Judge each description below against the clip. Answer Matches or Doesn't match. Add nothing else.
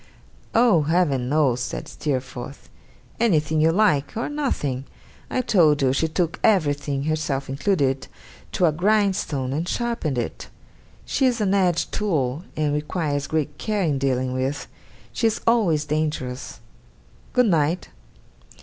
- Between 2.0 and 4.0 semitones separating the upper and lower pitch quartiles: Doesn't match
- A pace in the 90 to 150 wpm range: Matches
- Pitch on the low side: Doesn't match